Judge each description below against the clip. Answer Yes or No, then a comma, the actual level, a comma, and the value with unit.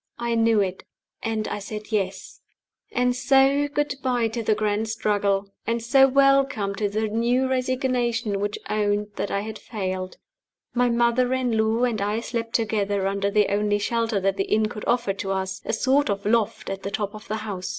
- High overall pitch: Yes, high, 220 Hz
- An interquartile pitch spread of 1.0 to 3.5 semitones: Yes, average, 2.9 semitones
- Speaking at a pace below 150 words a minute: No, average, 190 wpm